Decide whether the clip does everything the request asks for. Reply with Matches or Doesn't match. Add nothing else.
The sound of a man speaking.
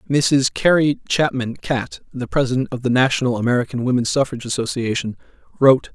Matches